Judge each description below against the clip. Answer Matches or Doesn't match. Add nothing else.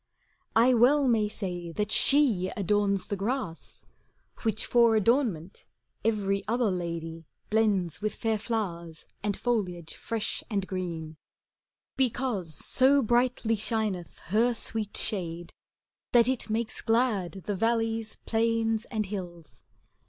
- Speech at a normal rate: Doesn't match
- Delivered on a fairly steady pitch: Doesn't match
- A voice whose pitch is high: Matches